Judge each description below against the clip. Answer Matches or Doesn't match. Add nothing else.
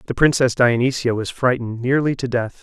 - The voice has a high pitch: Doesn't match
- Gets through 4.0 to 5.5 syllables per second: Doesn't match